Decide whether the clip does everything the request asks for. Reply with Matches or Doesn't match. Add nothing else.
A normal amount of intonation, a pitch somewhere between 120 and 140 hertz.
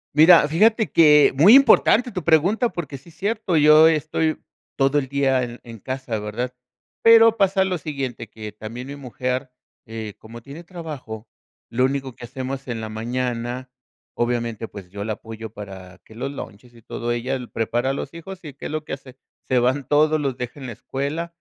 Matches